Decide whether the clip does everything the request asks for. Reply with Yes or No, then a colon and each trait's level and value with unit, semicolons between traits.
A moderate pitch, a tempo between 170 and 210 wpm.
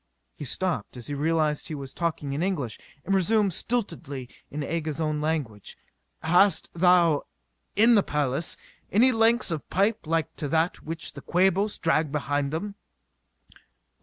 No: medium, 160 Hz; average, 150 wpm